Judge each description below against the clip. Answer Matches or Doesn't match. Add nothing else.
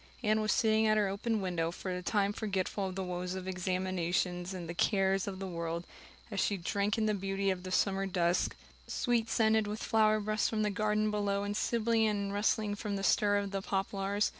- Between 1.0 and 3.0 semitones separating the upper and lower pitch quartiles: Matches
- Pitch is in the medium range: Doesn't match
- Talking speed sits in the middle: Doesn't match